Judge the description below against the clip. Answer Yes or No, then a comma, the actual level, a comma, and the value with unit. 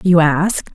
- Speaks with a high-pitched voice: No, medium, 170 Hz